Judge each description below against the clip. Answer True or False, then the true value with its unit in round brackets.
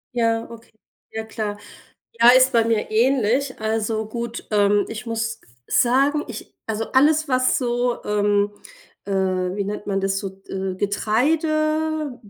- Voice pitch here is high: True (225 Hz)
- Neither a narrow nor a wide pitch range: True (3.6 semitones)